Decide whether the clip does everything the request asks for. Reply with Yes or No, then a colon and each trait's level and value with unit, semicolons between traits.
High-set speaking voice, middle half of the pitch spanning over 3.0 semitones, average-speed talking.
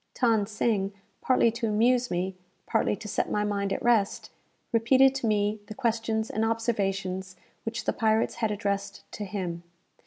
No: high, 215 Hz; narrow, 2.4 semitones; average, 160 wpm